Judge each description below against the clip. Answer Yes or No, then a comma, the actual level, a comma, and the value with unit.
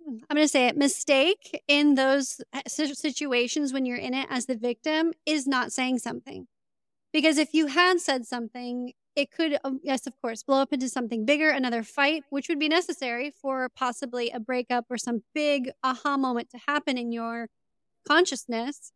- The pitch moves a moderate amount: Yes, average, 3.1 semitones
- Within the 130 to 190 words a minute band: Yes, average, 175 wpm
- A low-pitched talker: No, very high, 270 Hz